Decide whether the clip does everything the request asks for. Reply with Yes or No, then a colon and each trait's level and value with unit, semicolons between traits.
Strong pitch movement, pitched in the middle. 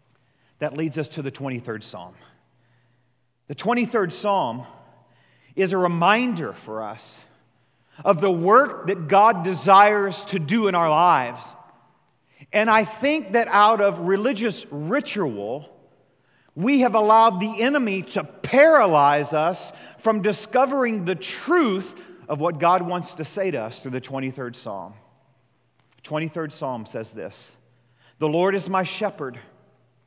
Yes: wide, 8.2 semitones; medium, 175 Hz